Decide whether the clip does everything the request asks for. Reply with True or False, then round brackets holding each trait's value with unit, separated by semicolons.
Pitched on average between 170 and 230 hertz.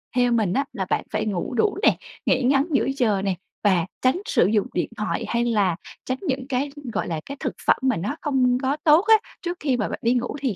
False (250 Hz)